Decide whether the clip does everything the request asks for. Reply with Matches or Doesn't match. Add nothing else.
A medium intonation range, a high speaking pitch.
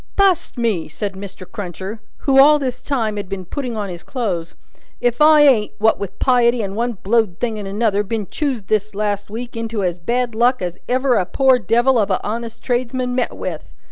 Matches